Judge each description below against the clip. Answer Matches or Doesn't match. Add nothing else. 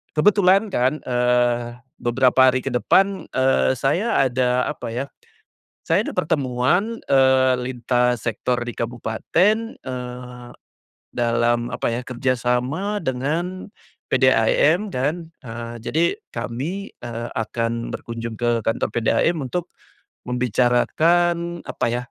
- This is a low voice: Matches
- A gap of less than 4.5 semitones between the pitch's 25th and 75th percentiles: Doesn't match